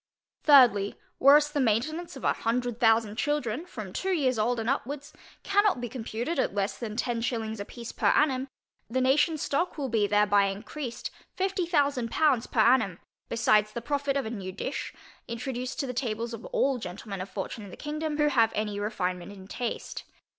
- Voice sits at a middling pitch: No, high, 240 Hz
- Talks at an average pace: Yes, average, 190 wpm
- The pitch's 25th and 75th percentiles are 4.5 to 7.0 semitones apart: Yes, average, 4.9 semitones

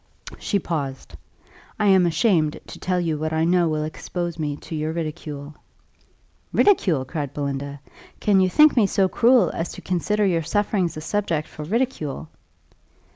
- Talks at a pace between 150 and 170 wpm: Yes, average, 160 wpm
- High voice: No, medium, 165 Hz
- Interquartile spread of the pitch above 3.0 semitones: Yes, average, 4.2 semitones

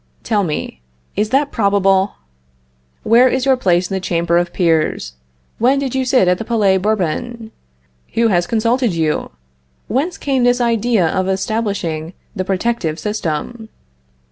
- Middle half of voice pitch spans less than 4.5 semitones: No, average, 5.2 semitones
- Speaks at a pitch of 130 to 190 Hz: No, high, 205 Hz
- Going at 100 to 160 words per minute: Yes, average, 145 wpm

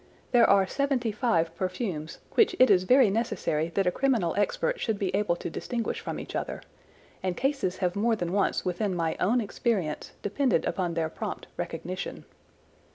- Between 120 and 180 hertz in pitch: No, high, 200 Hz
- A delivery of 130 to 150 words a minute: No, average, 170 wpm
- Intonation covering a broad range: No, average, 5.0 semitones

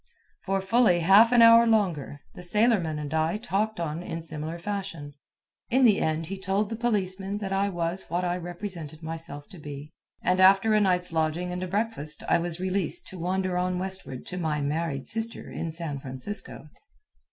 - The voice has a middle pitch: Yes, medium, 180 Hz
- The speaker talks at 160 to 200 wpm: Yes, average, 185 wpm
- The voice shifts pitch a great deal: No, average, 3.8 semitones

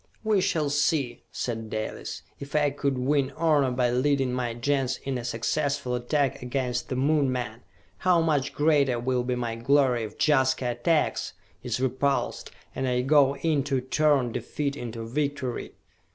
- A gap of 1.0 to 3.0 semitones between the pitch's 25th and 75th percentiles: Yes, average, 2.7 semitones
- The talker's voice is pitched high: No, low, 135 Hz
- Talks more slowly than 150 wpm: No, average, 160 wpm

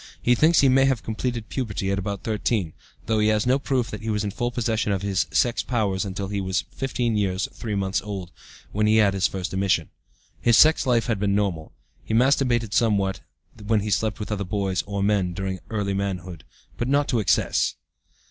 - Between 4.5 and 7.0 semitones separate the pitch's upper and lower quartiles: No, average, 3.2 semitones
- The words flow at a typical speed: No, fast, 210 wpm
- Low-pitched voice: Yes, low, 105 Hz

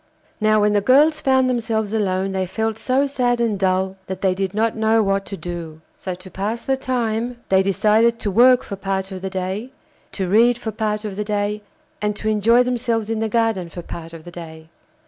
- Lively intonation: No, average, 3.3 semitones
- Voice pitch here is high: Yes, high, 210 Hz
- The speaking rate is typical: No, fast, 215 wpm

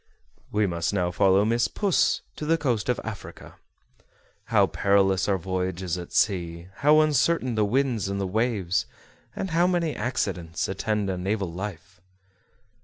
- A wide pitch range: No, average, 4.9 semitones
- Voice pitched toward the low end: Yes, low, 100 Hz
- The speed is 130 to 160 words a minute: Yes, average, 150 wpm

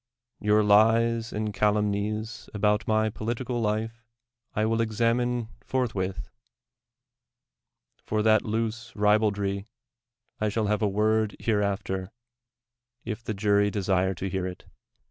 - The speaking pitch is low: Yes, low, 105 Hz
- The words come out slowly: Yes, slow, 120 wpm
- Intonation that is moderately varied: No, narrow, 1.7 semitones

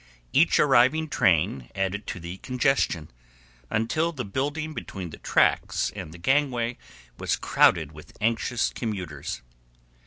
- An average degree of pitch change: No, wide, 7.9 semitones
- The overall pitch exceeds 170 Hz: No, low, 115 Hz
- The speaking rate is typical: No, slow, 125 wpm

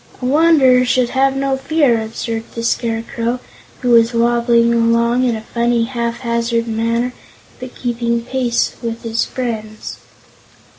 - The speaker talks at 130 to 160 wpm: Yes, slow, 135 wpm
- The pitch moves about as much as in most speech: No, narrow, 1.5 semitones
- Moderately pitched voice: No, high, 235 Hz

